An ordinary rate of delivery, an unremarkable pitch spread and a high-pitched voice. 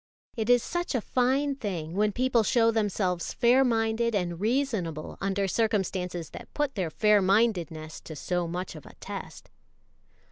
Yes: average, 155 wpm; average, 4.9 semitones; high, 210 Hz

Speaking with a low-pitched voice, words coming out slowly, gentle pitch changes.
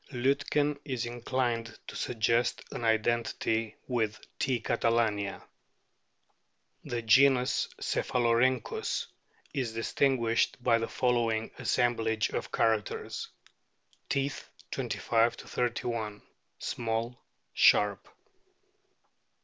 Yes: low, 115 Hz; slow, 80 wpm; narrow, 1.7 semitones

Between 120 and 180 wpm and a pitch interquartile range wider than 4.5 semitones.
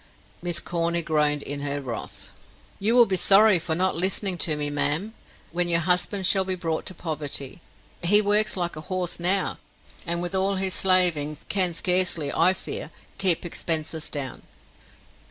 No: average, 165 wpm; average, 3.3 semitones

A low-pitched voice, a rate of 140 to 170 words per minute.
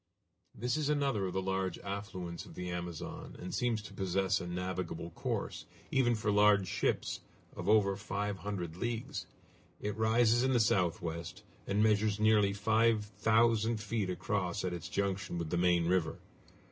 Yes: low, 100 Hz; average, 160 wpm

